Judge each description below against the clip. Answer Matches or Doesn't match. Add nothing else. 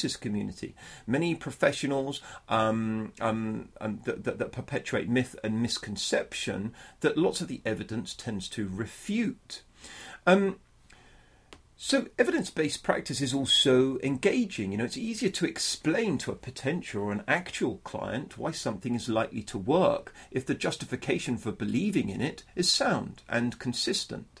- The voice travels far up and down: Matches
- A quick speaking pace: Doesn't match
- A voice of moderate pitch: Doesn't match